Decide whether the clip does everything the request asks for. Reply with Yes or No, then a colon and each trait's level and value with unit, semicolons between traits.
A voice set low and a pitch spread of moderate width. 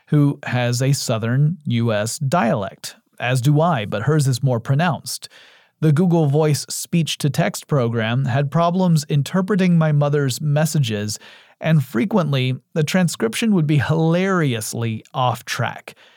No: medium, 150 Hz; average, 4.5 semitones